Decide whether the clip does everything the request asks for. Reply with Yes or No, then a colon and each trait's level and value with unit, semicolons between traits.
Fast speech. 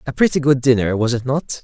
Yes: fast, 255 wpm